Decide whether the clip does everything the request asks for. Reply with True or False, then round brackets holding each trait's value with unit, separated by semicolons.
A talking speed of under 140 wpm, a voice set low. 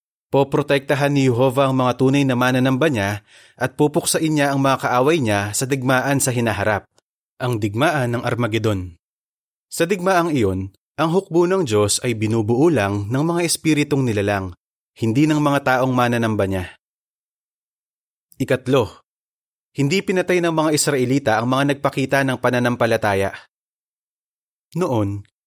True (125 wpm; 130 Hz)